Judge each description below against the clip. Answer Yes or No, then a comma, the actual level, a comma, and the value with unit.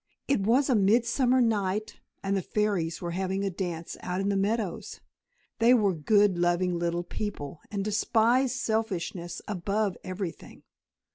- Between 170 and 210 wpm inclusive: No, average, 145 wpm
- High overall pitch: Yes, high, 200 Hz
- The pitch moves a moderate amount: Yes, average, 3.6 semitones